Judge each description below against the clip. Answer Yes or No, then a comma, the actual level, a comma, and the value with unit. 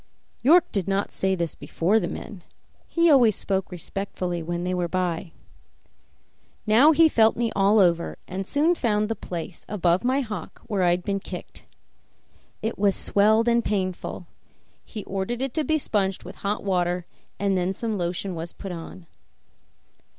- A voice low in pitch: No, high, 195 Hz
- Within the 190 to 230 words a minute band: No, average, 165 wpm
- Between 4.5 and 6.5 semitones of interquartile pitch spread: No, average, 3.7 semitones